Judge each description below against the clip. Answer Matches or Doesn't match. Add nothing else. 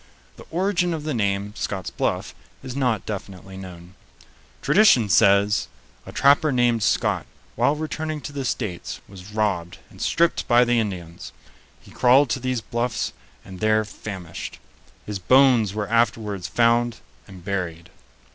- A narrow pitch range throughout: Doesn't match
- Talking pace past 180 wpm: Doesn't match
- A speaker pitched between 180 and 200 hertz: Doesn't match